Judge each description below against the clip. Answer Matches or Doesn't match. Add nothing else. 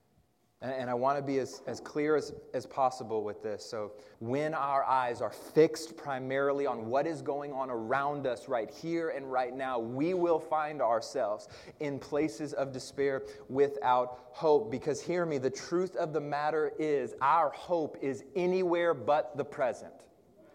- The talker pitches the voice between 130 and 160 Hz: Matches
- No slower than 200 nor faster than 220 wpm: Doesn't match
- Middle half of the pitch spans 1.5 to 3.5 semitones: Matches